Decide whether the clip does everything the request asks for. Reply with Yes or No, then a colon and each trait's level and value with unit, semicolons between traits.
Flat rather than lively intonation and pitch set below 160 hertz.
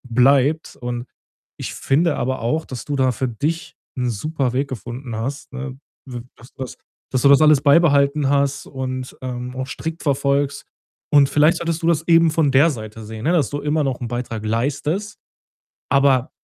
No: average, 3.1 semitones; medium, 140 Hz